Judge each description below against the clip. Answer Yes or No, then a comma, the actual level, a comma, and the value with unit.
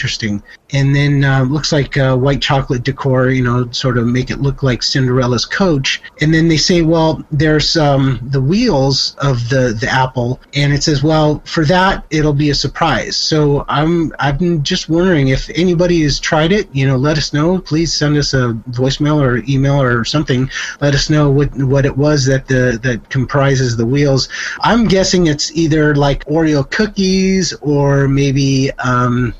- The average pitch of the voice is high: No, medium, 140 Hz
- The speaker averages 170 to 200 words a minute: Yes, average, 185 wpm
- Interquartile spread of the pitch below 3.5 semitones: Yes, average, 2.8 semitones